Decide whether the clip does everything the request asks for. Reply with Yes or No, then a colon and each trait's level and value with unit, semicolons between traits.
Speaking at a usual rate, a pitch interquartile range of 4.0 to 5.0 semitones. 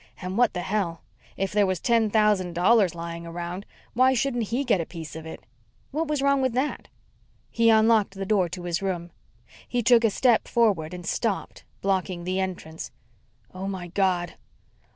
Yes: average, 180 wpm; average, 4.7 semitones